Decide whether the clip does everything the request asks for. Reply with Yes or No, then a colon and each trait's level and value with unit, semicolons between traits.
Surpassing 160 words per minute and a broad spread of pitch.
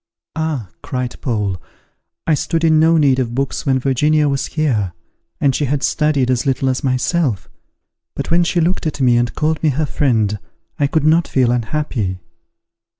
No: average, 175 wpm; average, 4.0 semitones